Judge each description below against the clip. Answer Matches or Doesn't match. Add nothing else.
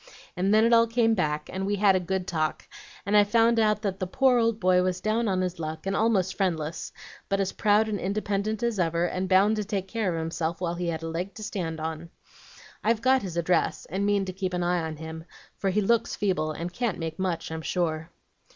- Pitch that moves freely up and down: Doesn't match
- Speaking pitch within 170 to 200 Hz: Matches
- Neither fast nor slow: Doesn't match